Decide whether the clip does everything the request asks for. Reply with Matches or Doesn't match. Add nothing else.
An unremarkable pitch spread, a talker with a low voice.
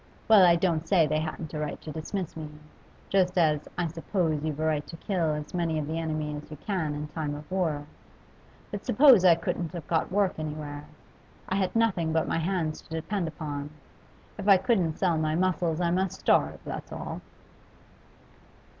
Doesn't match